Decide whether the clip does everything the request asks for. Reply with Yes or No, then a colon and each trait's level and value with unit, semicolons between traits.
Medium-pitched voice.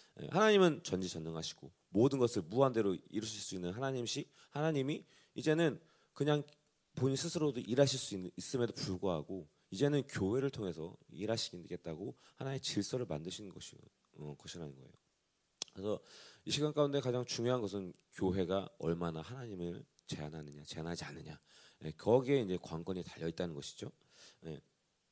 No: low, 110 Hz